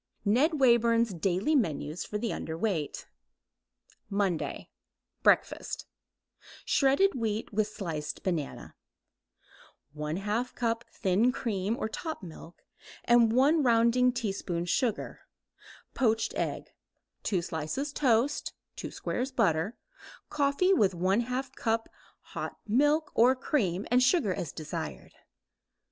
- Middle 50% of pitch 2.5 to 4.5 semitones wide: No, average, 5.3 semitones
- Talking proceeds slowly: Yes, slow, 105 wpm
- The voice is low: No, high, 225 Hz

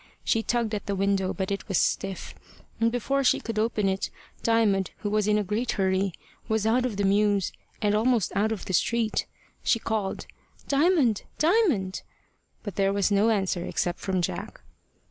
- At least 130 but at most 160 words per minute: No, average, 180 wpm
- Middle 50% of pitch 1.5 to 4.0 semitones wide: Yes, average, 2.8 semitones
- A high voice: Yes, high, 210 Hz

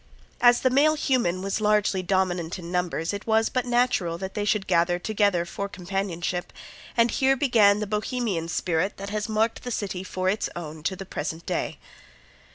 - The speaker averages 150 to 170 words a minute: No, average, 180 wpm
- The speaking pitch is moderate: No, high, 195 Hz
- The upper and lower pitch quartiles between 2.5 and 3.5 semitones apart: No, average, 3.9 semitones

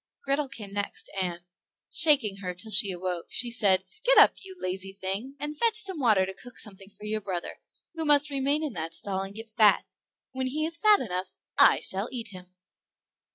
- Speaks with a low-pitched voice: No, high, 215 Hz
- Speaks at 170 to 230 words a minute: Yes, average, 200 wpm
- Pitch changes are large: Yes, wide, 6.8 semitones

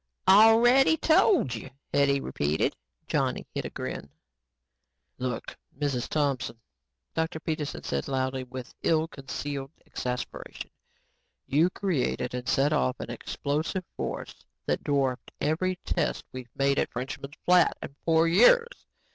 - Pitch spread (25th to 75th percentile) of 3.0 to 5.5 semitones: Yes, average, 4.5 semitones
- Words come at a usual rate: No, slow, 130 wpm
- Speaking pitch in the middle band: Yes, medium, 145 Hz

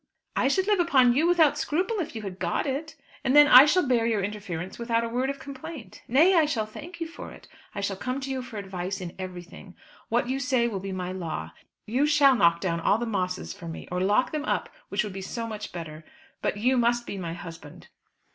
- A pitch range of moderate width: No, wide, 6.7 semitones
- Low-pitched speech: No, high, 230 Hz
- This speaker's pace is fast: Yes, fast, 235 wpm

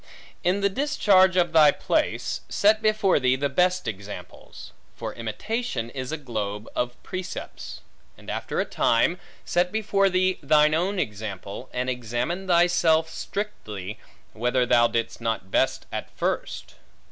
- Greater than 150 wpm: No, average, 140 wpm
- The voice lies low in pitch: No, medium, 155 Hz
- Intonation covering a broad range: Yes, wide, 7.9 semitones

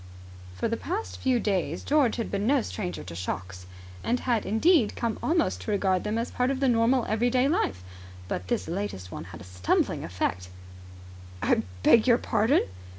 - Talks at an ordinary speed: Yes, average, 180 wpm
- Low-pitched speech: No, high, 220 Hz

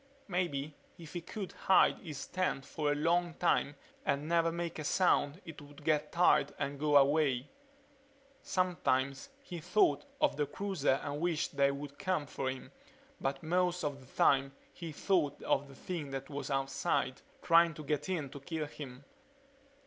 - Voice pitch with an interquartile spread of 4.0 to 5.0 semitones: No, average, 3.6 semitones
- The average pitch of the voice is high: No, medium, 150 Hz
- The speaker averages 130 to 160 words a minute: No, average, 170 wpm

